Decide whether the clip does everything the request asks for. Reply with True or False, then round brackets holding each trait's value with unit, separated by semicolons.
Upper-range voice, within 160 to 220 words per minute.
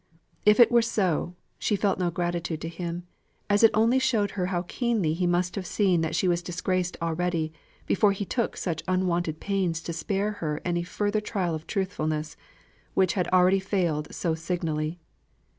False (180 Hz; 175 wpm)